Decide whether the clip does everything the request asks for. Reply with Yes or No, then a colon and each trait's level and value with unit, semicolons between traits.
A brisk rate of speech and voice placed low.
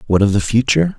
Yes: fast, 245 wpm; low, 120 Hz